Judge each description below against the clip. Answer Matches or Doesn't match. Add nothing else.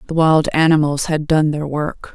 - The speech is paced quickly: Doesn't match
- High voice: Doesn't match